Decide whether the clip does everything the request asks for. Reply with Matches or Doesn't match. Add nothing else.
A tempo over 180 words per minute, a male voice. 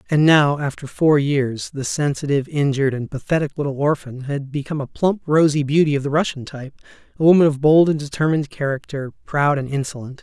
Matches